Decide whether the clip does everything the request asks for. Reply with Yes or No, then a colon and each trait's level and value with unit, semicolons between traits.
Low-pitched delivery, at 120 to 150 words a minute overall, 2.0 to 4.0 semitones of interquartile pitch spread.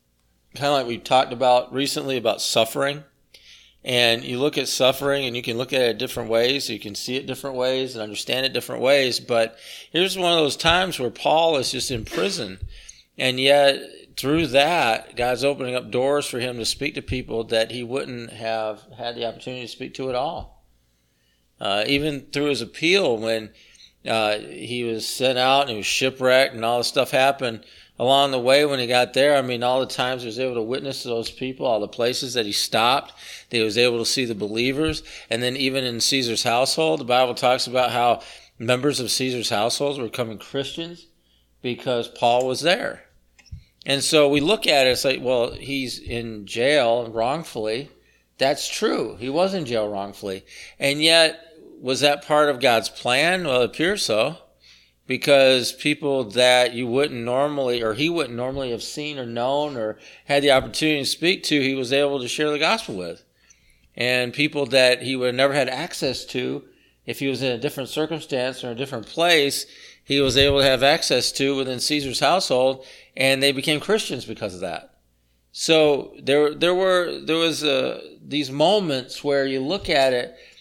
No: low, 130 Hz; average, 195 wpm; average, 3.3 semitones